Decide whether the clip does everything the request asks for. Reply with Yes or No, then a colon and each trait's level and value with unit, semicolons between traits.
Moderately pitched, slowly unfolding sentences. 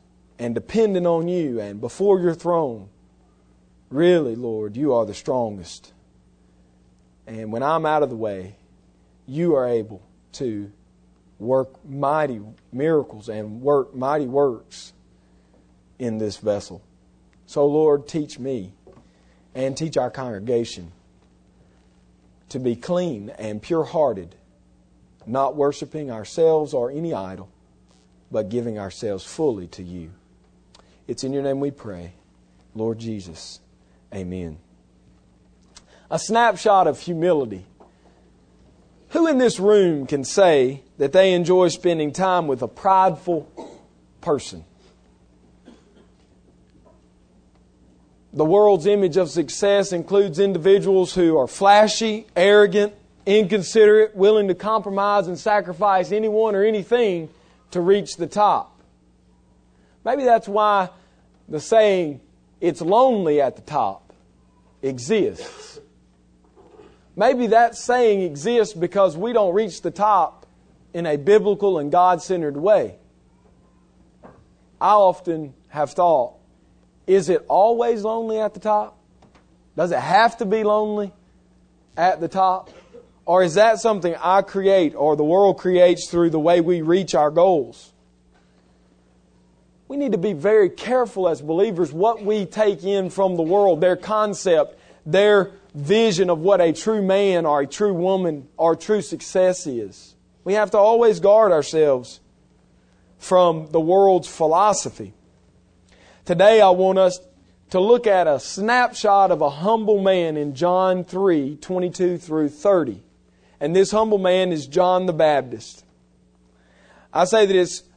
Yes: medium, 155 Hz; slow, 125 wpm